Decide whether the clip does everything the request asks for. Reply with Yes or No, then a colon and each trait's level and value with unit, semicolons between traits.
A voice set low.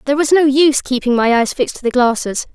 No: very high, 265 Hz